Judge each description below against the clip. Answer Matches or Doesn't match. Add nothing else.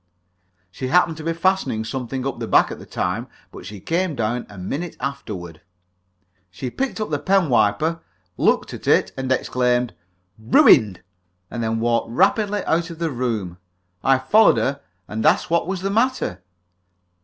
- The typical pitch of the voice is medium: Doesn't match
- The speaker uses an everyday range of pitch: Doesn't match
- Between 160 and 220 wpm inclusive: Matches